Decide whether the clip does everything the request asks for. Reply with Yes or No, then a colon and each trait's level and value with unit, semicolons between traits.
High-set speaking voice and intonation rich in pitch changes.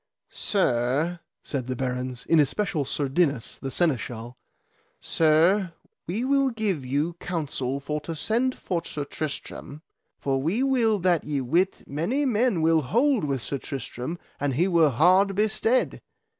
No: medium, 160 Hz; wide, 6.1 semitones